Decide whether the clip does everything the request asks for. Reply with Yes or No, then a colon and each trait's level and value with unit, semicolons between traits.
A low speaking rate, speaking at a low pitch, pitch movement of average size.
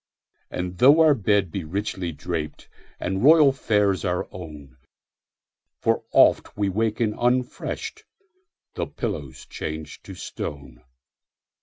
No: slow, 100 wpm; very low, 95 Hz; wide, 7.5 semitones